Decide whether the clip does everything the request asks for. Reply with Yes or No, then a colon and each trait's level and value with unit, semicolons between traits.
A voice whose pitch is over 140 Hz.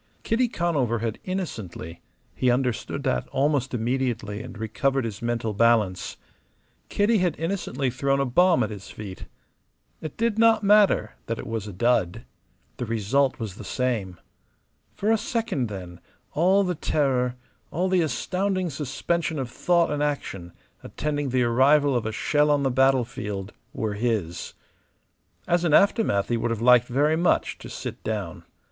No: low, 130 Hz